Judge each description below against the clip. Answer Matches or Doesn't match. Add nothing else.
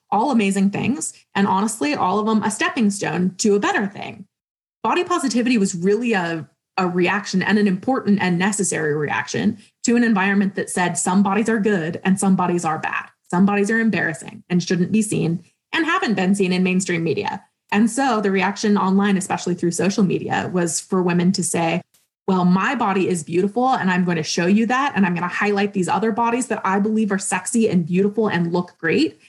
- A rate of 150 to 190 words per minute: Doesn't match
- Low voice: Doesn't match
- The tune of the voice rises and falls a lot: Doesn't match